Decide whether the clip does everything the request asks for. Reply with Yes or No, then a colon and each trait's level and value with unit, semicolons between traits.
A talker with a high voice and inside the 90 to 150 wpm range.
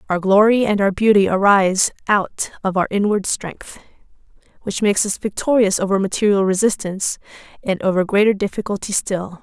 Yes: high, 200 Hz; average, 145 wpm